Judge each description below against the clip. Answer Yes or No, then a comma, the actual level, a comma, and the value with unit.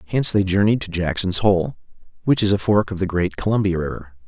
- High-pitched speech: No, very low, 95 Hz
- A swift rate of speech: Yes, fast, 210 wpm